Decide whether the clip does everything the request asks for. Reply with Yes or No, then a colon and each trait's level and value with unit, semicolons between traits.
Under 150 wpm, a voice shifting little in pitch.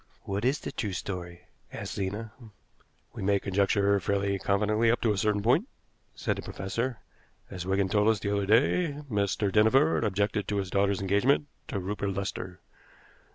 No: average, 165 wpm; narrow, 1.9 semitones